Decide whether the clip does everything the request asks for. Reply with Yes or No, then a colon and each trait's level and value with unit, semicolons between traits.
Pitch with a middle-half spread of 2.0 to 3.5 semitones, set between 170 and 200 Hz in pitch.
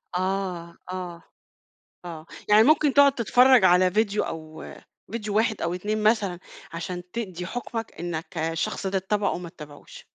No: average, 4.0 semitones; medium, 185 Hz